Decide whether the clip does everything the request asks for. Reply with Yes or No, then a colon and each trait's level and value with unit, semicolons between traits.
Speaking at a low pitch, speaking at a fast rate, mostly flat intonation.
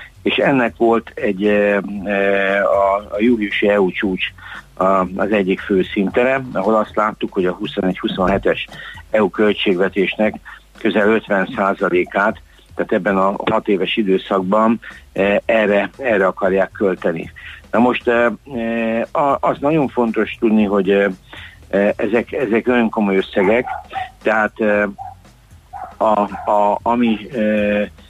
No: low, 105 Hz; slow, 105 wpm; narrow, 2.3 semitones